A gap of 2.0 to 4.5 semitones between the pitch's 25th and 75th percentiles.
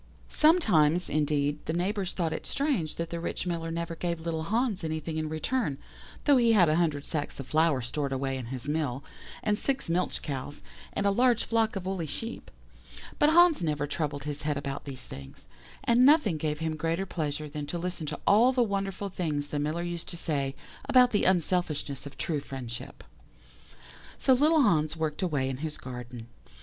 No: average, 5.1 semitones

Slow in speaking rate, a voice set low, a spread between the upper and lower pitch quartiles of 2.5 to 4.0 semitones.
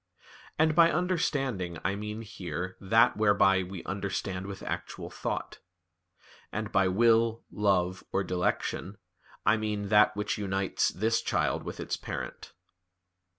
Yes: slow, 130 wpm; low, 100 Hz; average, 2.8 semitones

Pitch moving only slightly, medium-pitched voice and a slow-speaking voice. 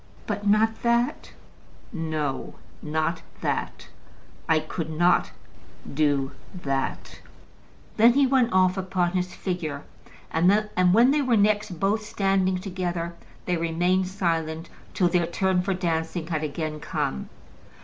No: average, 3.7 semitones; medium, 180 Hz; slow, 125 wpm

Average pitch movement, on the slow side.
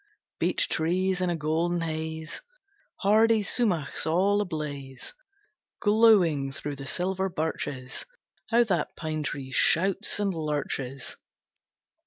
Yes: average, 4.3 semitones; slow, 110 wpm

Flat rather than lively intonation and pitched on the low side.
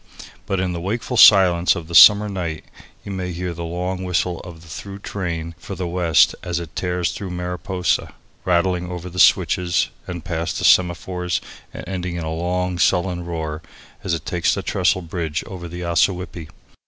Yes: narrow, 1.3 semitones; very low, 90 Hz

